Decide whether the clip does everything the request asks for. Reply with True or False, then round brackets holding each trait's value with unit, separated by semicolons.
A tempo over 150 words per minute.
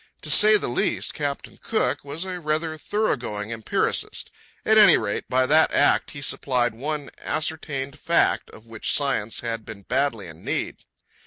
True (165 wpm)